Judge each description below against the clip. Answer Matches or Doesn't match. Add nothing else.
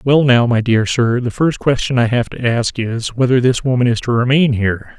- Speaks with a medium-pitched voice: Doesn't match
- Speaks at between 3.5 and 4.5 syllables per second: Doesn't match